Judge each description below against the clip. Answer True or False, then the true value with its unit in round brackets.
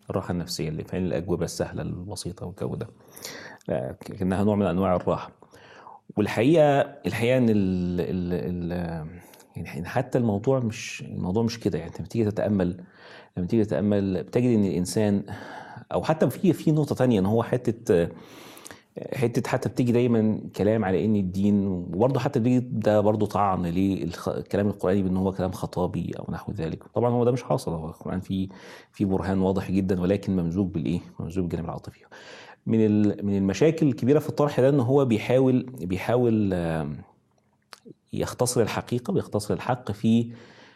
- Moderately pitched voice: False (105 Hz)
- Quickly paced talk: True (150 wpm)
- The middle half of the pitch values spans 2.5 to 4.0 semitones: False (4.5 semitones)